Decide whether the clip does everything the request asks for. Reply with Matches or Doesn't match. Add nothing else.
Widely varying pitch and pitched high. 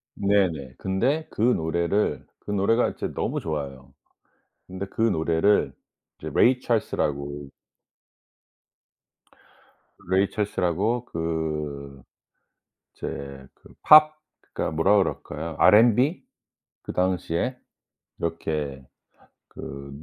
Doesn't match